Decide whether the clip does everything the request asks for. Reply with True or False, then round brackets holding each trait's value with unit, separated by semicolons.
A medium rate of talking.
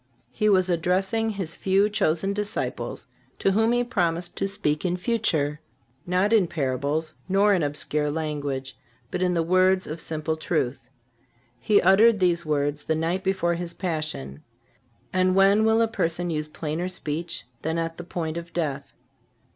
True (160 wpm)